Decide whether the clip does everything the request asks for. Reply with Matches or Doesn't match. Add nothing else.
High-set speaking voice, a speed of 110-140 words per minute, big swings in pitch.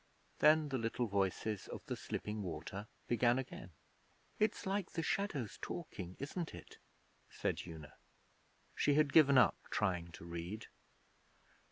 Doesn't match